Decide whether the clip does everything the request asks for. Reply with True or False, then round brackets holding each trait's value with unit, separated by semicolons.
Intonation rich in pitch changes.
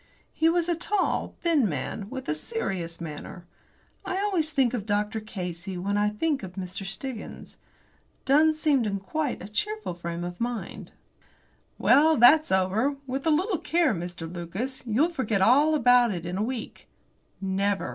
True (8.3 semitones)